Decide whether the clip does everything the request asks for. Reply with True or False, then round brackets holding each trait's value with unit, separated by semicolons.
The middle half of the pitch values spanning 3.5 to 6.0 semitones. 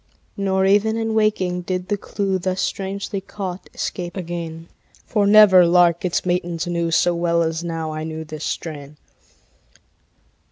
False (2.6 semitones)